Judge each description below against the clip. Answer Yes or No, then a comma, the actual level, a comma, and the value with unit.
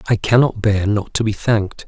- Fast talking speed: Yes, fast, 225 wpm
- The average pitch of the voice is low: Yes, low, 105 Hz